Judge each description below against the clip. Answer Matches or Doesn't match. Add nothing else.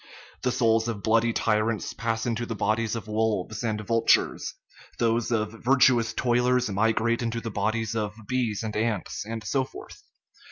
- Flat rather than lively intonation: Matches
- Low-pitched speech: Matches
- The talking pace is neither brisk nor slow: Matches